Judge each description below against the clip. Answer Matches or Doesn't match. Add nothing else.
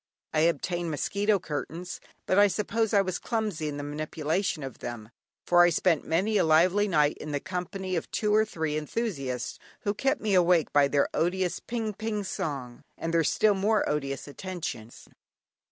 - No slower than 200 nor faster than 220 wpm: Doesn't match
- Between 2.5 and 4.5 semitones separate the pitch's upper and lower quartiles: Doesn't match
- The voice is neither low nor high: Matches